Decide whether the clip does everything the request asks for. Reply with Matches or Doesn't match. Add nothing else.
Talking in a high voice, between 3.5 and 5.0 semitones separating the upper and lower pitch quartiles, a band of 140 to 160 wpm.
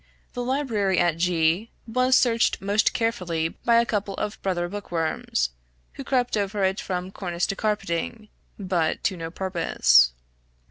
Matches